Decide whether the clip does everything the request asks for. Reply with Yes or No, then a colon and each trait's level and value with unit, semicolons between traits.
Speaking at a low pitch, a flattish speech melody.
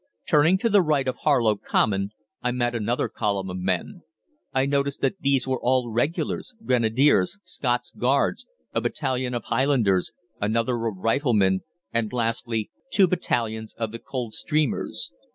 No: low, 120 Hz; average, 3.9 semitones